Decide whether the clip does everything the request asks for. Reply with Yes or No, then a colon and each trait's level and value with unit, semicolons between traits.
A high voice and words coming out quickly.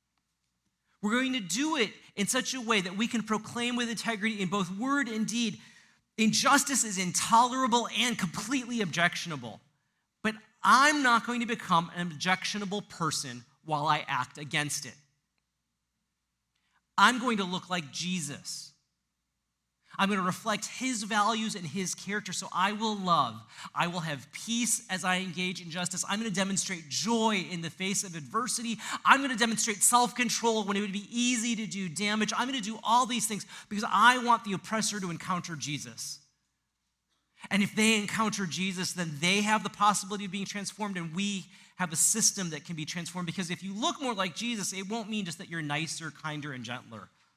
No: high, 195 Hz; average, 185 wpm